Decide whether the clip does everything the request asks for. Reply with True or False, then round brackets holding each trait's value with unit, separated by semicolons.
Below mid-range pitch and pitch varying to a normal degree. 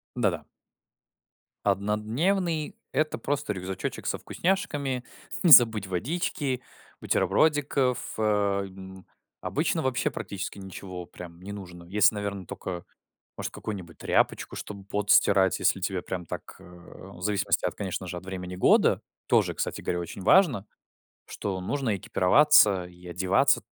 False (100 Hz; 5.7 semitones)